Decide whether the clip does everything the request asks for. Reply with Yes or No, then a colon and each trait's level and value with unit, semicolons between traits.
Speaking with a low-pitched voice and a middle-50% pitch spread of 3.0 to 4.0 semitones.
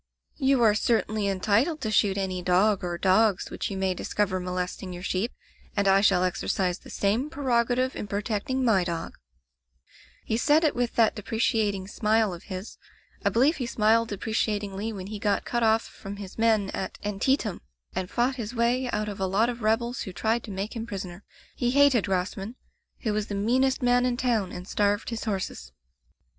No: high, 210 Hz; average, 3.5 semitones